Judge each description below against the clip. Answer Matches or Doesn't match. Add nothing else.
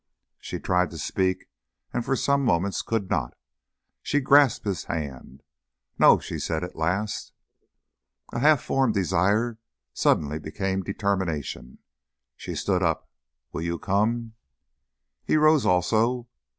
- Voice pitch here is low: Matches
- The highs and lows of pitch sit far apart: Matches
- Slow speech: Matches